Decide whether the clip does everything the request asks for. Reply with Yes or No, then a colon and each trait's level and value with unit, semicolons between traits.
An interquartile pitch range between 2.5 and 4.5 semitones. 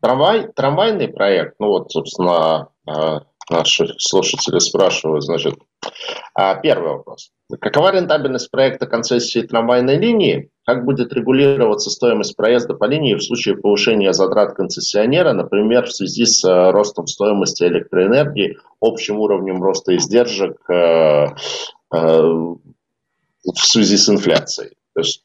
No: wide, 5.5 semitones